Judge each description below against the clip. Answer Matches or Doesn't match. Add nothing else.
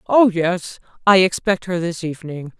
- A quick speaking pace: Doesn't match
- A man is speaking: Doesn't match